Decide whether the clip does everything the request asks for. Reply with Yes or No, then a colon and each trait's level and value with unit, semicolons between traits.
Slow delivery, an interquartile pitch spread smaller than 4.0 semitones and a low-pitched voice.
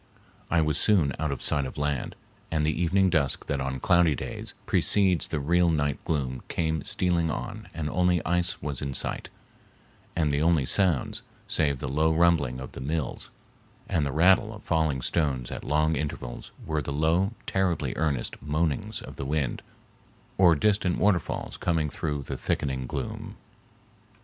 No: average, 165 wpm; average, 3.6 semitones; very low, 80 Hz